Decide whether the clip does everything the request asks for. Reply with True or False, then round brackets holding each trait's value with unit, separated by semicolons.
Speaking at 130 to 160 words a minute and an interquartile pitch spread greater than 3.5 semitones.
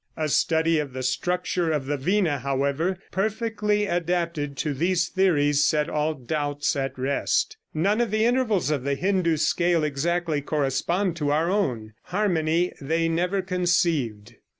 True (150 wpm; 4.0 semitones)